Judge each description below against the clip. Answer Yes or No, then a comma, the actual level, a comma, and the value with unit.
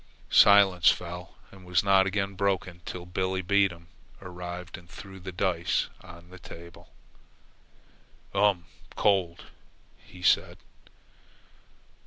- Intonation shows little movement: Yes, narrow, 1.9 semitones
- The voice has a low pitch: Yes, very low, 90 Hz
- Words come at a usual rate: No, slow, 115 wpm